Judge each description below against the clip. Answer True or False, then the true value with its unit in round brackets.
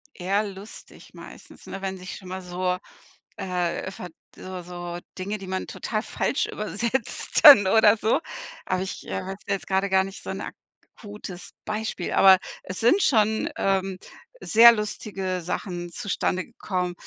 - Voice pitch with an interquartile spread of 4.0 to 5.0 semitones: False (2.4 semitones)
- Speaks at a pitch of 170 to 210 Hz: True (190 Hz)